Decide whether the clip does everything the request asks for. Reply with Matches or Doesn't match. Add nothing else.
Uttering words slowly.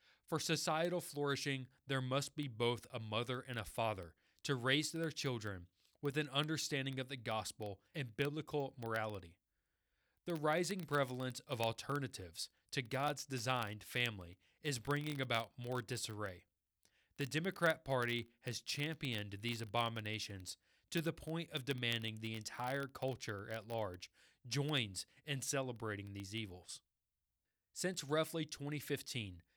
Matches